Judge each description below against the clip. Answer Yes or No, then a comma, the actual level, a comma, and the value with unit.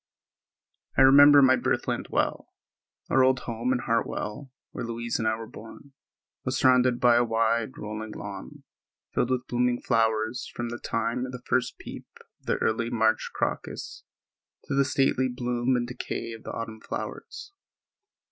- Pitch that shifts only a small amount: Yes, narrow, 2.2 semitones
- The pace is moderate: Yes, average, 160 wpm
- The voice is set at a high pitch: No, low, 120 Hz